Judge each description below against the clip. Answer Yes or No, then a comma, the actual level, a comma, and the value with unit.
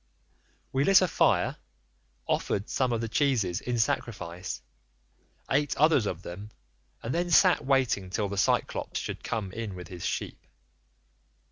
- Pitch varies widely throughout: Yes, wide, 6.2 semitones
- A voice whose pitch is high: No, low, 115 Hz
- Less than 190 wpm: Yes, average, 145 wpm